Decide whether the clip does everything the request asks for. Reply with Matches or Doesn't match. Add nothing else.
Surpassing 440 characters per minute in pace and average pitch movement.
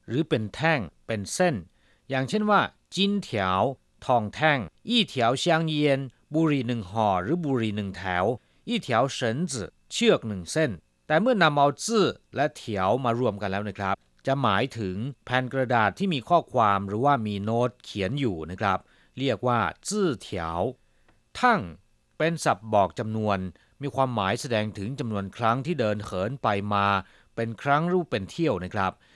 Doesn't match